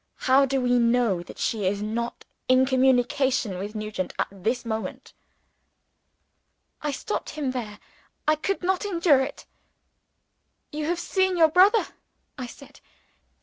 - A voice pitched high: Yes, very high, 260 Hz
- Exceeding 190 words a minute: No, average, 140 wpm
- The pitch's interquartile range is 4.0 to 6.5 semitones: Yes, wide, 5.4 semitones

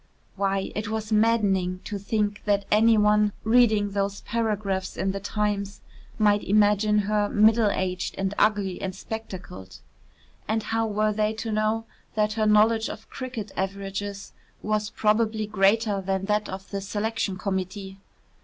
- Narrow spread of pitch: Yes, narrow, 1.7 semitones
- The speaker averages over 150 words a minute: No, average, 145 wpm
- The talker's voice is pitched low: No, high, 210 Hz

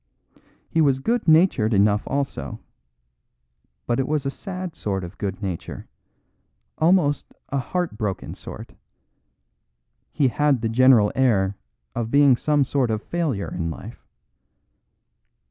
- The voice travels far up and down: Yes, wide, 5.9 semitones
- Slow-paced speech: Yes, slow, 130 wpm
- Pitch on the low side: Yes, low, 130 Hz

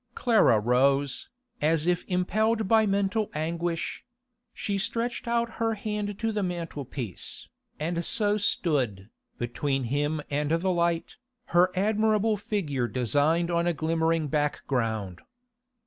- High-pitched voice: No, medium, 170 Hz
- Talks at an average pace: No, slow, 125 wpm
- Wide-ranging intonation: Yes, wide, 6.2 semitones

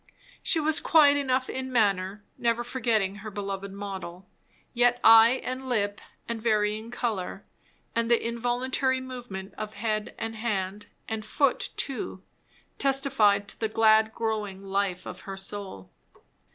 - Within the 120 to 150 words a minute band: Yes, average, 140 wpm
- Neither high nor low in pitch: No, high, 220 Hz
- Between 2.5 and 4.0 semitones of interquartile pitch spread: Yes, average, 3.5 semitones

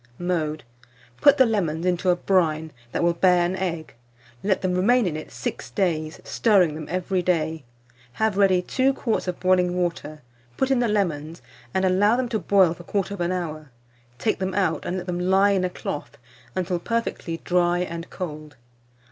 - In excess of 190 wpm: No, average, 180 wpm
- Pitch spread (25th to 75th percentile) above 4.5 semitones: No, average, 2.7 semitones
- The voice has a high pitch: No, medium, 180 Hz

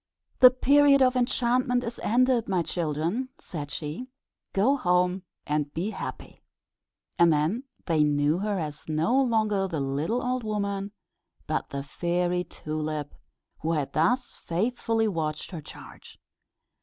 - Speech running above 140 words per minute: No, slow, 135 wpm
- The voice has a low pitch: No, medium, 185 Hz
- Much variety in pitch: Yes, wide, 7.6 semitones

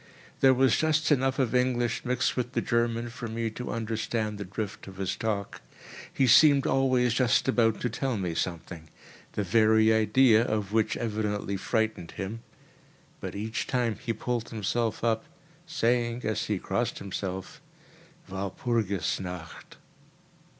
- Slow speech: No, average, 145 wpm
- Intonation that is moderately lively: Yes, average, 3.1 semitones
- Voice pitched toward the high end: No, low, 115 Hz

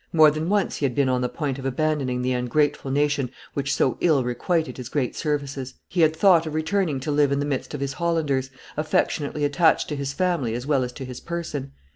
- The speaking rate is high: Yes, fast, 225 wpm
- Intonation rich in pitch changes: No, average, 3.0 semitones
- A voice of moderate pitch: Yes, medium, 145 Hz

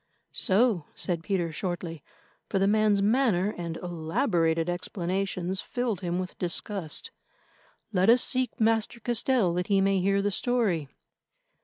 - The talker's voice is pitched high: Yes, high, 195 Hz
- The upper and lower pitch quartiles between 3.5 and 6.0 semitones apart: Yes, average, 3.8 semitones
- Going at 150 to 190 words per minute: No, slow, 135 wpm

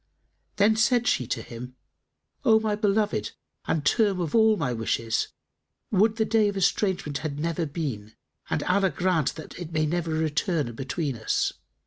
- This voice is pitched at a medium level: Yes, medium, 170 Hz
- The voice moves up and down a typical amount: No, wide, 6.4 semitones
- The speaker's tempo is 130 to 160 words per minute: Yes, average, 155 wpm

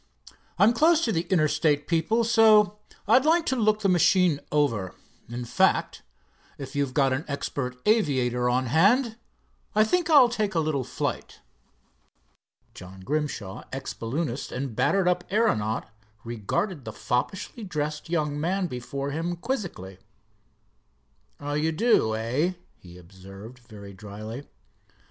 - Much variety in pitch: Yes, wide, 8.6 semitones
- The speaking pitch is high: No, medium, 150 Hz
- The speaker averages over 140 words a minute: No, slow, 135 wpm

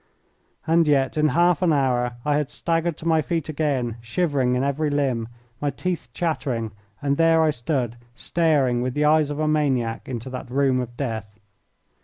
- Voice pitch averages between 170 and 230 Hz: No, medium, 140 Hz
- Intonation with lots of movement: No, average, 3.9 semitones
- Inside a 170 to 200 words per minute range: Yes, average, 180 wpm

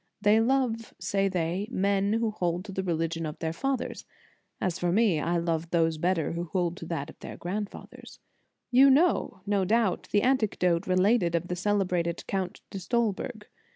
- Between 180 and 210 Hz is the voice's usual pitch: Yes, high, 190 Hz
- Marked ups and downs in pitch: No, average, 3.9 semitones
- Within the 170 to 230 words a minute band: Yes, average, 180 wpm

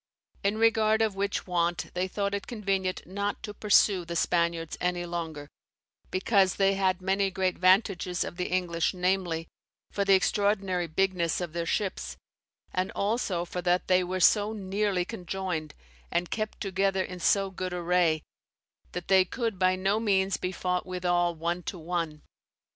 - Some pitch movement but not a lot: No, narrow, 2.0 semitones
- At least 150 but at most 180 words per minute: Yes, average, 160 wpm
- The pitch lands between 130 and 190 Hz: Yes, medium, 185 Hz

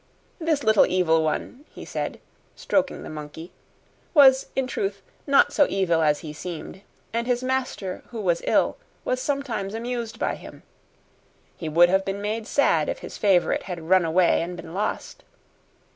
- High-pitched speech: Yes, high, 195 Hz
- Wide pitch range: Yes, wide, 6.7 semitones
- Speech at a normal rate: Yes, average, 165 wpm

